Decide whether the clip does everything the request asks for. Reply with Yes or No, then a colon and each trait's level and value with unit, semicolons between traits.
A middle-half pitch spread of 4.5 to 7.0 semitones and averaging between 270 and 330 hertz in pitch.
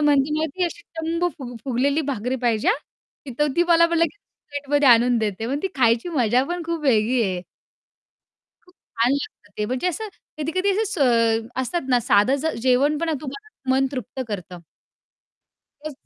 Yes: average, 5.3 semitones; very high, 275 Hz